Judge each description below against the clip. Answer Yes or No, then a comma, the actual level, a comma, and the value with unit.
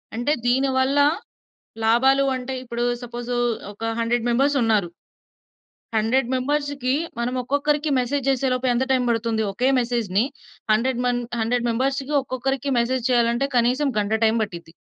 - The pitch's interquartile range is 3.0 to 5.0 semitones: No, narrow, 2.4 semitones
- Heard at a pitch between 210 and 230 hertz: No, high, 245 Hz